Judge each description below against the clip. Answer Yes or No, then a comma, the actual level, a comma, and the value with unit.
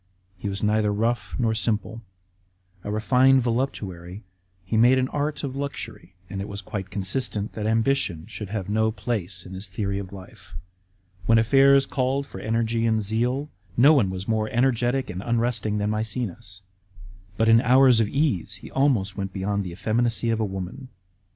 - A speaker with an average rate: Yes, average, 170 wpm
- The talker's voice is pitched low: Yes, low, 110 Hz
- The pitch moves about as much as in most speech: Yes, average, 3.8 semitones